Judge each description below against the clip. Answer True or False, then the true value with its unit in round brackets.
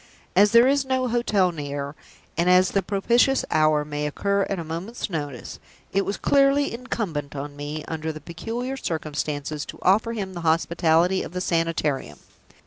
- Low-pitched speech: False (175 Hz)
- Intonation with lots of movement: True (6.1 semitones)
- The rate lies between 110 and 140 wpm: False (165 wpm)